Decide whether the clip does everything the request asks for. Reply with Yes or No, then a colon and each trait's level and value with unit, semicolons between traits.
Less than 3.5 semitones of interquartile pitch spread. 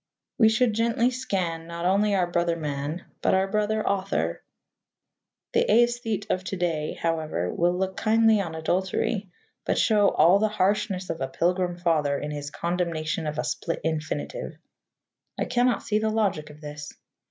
No: average, 4.7 semitones